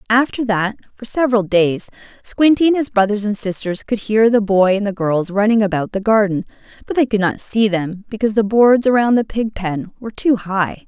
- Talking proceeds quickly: Yes, fast, 210 wpm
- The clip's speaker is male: No, female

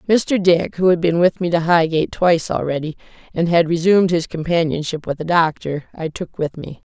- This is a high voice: No, medium, 165 Hz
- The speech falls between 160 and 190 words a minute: No, average, 200 wpm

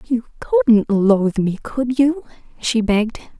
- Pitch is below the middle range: No, high, 225 Hz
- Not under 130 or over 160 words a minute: Yes, average, 140 wpm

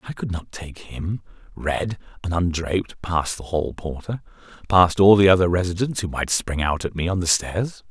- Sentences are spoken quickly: No, average, 195 wpm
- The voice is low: Yes, very low, 90 Hz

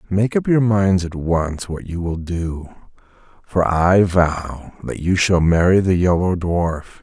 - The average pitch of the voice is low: Yes, very low, 90 Hz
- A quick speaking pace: No, average, 170 wpm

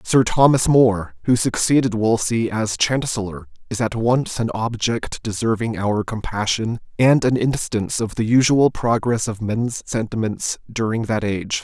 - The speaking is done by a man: Yes, male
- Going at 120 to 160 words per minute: Yes, average, 150 wpm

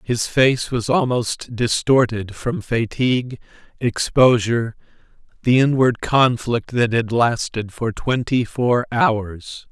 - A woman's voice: No, male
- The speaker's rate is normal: No, slow, 110 wpm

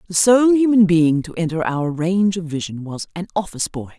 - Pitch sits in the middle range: Yes, medium, 175 Hz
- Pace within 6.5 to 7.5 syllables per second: No, 5.6 syllables/s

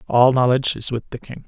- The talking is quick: Yes, fast, 245 wpm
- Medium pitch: No, low, 125 Hz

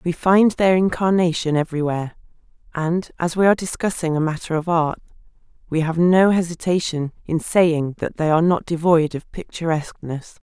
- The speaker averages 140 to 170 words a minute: Yes, average, 155 wpm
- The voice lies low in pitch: No, medium, 170 Hz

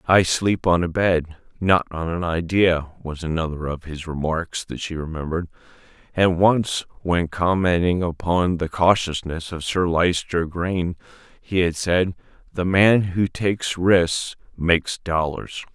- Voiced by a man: Yes, male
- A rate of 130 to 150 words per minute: Yes, average, 145 wpm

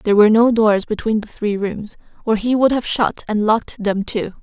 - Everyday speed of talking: No, fast, 230 wpm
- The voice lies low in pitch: No, high, 215 Hz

